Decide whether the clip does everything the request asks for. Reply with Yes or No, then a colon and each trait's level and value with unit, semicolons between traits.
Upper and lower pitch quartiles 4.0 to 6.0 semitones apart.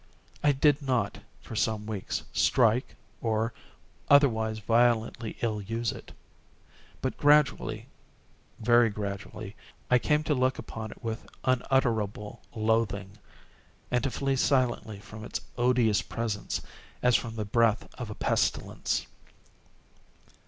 No: average, 2.7 semitones